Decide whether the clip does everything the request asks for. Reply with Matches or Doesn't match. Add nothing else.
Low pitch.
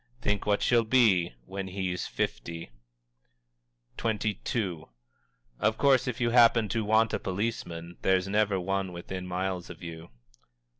Matches